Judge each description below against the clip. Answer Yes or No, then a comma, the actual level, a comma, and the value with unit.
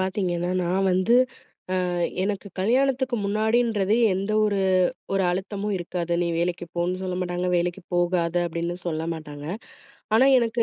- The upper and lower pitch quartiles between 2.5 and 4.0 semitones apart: Yes, average, 3.1 semitones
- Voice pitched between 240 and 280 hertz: No, medium, 185 Hz